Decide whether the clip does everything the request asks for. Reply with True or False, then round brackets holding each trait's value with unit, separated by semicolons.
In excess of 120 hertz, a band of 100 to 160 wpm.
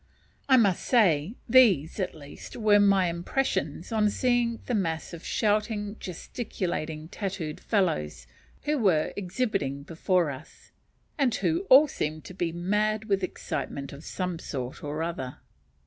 True (185 Hz; 140 wpm)